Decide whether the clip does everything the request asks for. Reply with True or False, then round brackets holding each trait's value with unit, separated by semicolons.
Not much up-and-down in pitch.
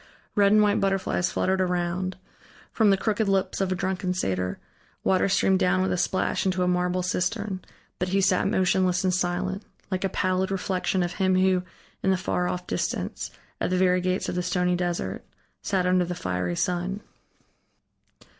True (1.1 semitones)